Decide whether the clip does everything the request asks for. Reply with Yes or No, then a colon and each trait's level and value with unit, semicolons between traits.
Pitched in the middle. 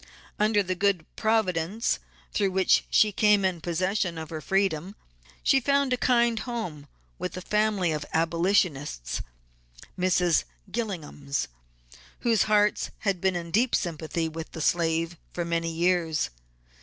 Yes: medium, 180 Hz